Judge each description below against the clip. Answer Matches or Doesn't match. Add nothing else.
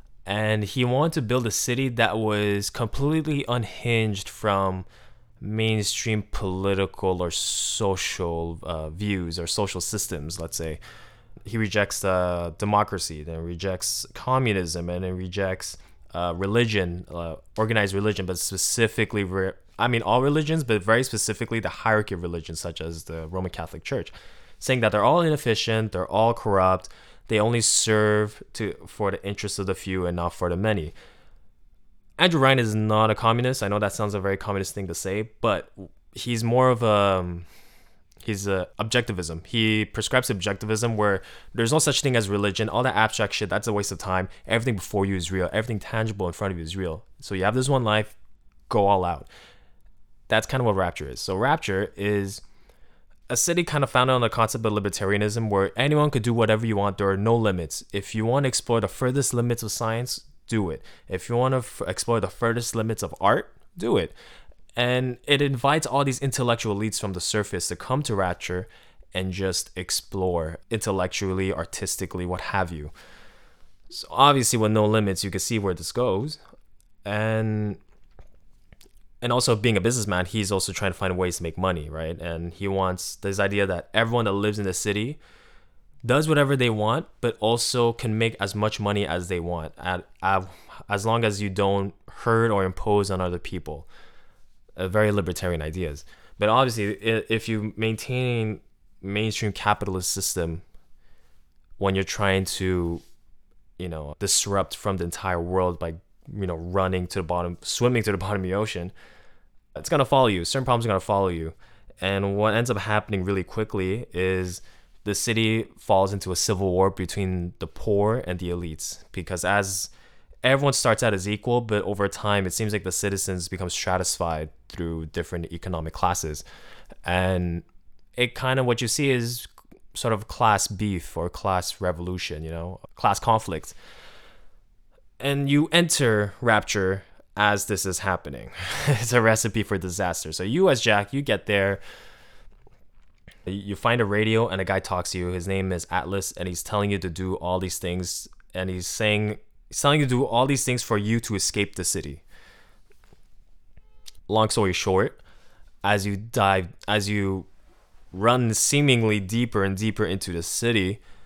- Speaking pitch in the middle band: Doesn't match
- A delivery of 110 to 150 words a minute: Doesn't match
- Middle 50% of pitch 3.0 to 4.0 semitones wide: Matches